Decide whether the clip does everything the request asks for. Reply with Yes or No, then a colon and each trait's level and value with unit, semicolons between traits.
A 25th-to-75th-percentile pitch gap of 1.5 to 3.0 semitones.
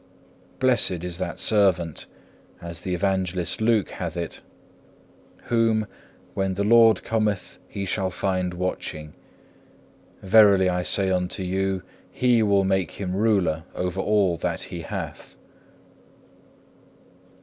Yes: narrow, 2.6 semitones